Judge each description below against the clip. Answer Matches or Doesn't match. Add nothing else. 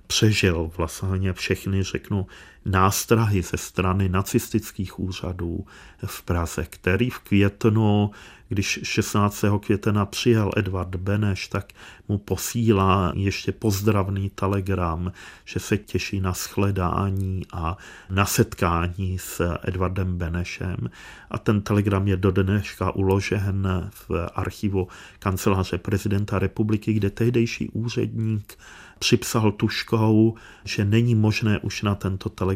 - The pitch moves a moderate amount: Doesn't match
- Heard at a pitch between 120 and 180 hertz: Doesn't match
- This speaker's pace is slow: Matches